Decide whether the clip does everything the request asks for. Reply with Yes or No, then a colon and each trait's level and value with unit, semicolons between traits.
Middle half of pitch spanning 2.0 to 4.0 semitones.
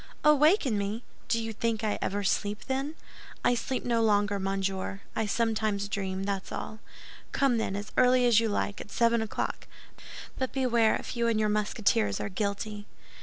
Yes: average, 2.7 semitones